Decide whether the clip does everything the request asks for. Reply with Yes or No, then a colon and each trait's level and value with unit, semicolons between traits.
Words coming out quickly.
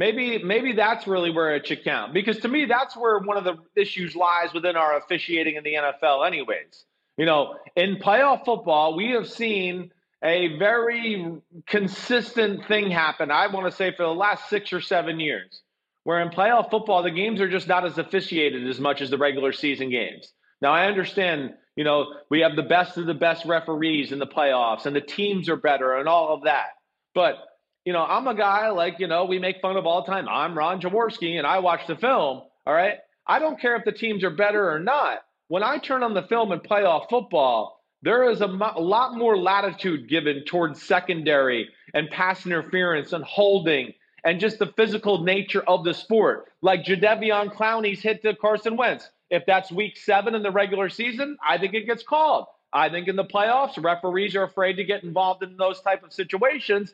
Yes: fast, 210 wpm